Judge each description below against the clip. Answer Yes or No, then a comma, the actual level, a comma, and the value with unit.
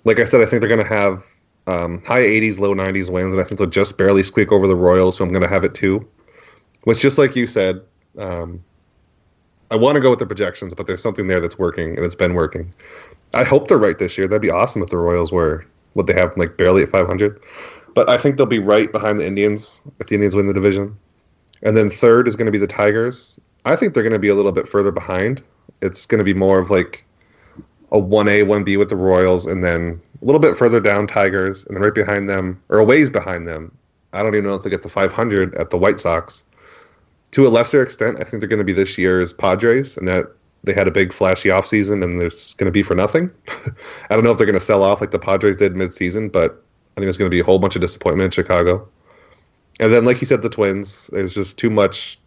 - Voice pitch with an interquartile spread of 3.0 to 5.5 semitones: No, narrow, 2.6 semitones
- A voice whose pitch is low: Yes, low, 100 Hz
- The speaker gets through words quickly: Yes, fast, 255 wpm